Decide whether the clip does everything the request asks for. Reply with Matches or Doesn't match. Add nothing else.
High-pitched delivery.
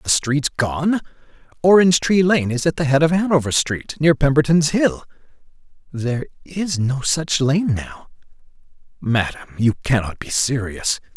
Doesn't match